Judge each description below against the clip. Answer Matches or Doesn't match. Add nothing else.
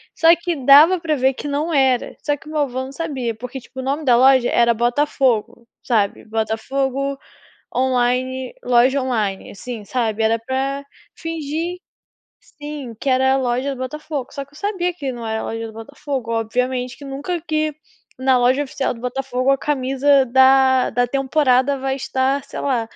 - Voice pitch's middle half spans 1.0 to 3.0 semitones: Matches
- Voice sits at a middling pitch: Doesn't match